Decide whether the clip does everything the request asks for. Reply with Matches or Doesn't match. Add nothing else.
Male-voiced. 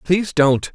Matches